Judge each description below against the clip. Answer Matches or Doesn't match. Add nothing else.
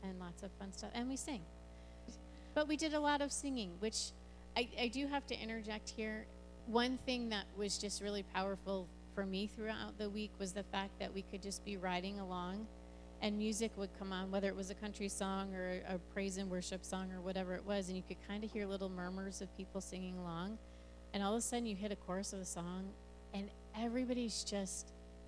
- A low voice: Doesn't match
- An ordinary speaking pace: Doesn't match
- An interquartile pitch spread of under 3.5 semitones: Matches